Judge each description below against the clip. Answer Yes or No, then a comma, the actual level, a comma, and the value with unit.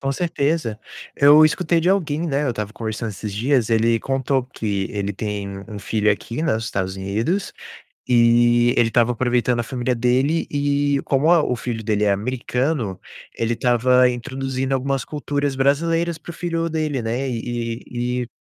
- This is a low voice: Yes, low, 125 Hz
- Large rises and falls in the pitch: No, average, 3.9 semitones